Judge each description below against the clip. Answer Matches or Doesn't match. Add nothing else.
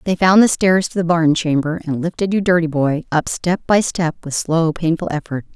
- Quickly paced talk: Matches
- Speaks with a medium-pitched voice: Matches